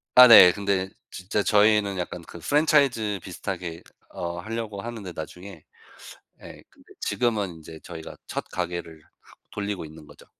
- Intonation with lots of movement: No, average, 3.8 semitones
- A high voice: No, low, 100 Hz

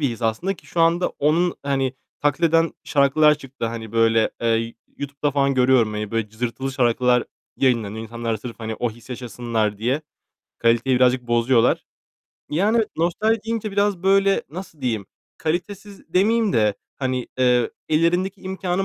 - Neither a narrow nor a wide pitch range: No, wide, 6.7 semitones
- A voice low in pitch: Yes, low, 130 Hz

